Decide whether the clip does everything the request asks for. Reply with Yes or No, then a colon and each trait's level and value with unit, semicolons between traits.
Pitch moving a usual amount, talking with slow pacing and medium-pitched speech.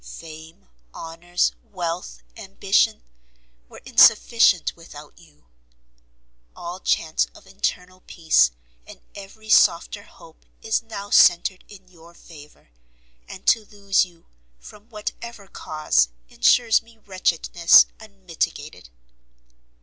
Yes: average, 3.9 semitones; slow, 105 wpm; medium, 180 Hz